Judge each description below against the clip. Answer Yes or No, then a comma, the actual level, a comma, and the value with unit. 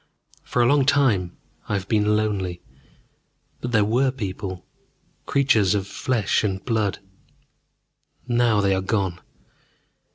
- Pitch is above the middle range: No, low, 105 Hz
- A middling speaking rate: No, slow, 125 wpm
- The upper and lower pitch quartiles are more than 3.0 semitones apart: Yes, average, 4.0 semitones